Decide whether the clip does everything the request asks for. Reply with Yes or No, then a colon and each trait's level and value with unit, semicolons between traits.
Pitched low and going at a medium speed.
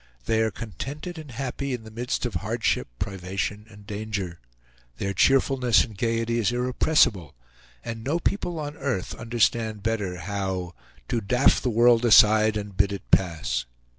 Yes: low, 110 Hz; average, 155 wpm